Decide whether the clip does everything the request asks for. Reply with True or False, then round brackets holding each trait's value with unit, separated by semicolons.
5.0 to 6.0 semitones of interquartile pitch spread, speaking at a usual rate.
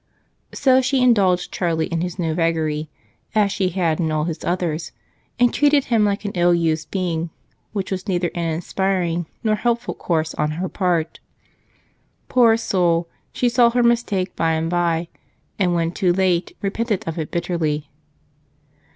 False (3.8 semitones; 160 wpm)